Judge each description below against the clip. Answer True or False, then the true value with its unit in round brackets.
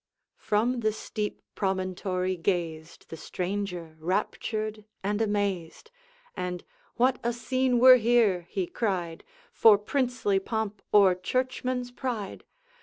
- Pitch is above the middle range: True (205 Hz)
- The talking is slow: True (110 wpm)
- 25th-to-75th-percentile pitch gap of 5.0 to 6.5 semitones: False (4.6 semitones)